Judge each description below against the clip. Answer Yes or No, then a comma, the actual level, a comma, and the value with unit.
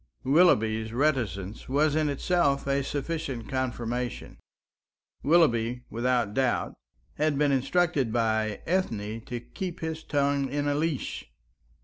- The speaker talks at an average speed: No, slow, 115 wpm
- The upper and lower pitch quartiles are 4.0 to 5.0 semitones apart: Yes, average, 4.5 semitones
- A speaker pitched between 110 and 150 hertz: Yes, low, 135 Hz